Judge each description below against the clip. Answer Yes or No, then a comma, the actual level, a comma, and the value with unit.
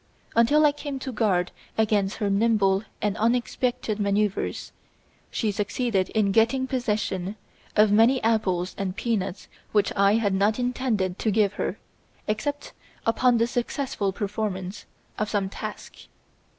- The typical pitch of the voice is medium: No, high, 215 Hz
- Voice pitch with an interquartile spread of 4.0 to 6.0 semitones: No, average, 3.0 semitones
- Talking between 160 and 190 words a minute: No, slow, 135 wpm